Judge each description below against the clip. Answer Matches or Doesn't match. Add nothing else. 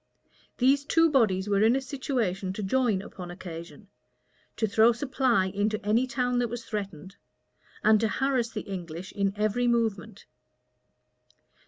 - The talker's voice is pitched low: Doesn't match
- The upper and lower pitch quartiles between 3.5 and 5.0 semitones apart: Matches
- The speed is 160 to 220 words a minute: Doesn't match